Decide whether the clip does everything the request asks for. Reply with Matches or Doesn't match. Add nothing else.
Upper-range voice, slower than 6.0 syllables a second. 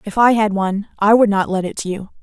Doesn't match